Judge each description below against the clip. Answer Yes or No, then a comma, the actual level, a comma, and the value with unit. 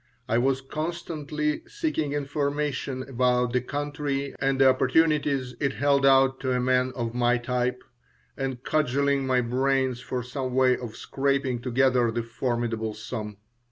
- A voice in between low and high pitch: No, low, 130 Hz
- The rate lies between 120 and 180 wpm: Yes, average, 145 wpm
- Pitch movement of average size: No, narrow, 2.2 semitones